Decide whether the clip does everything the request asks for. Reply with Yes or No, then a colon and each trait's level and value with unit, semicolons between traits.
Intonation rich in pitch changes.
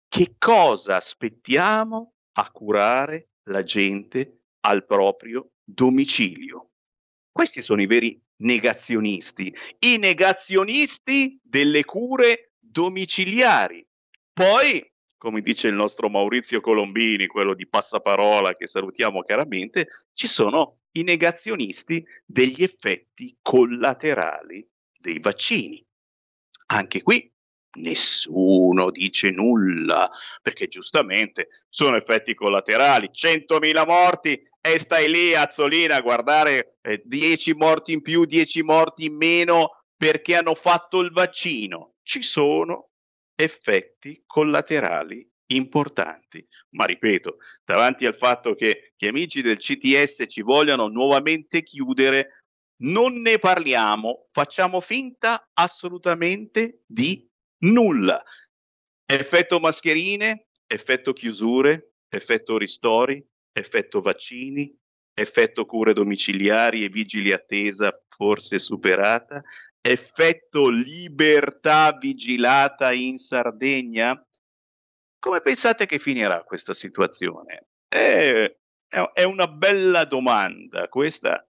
Yes: wide, 8.6 semitones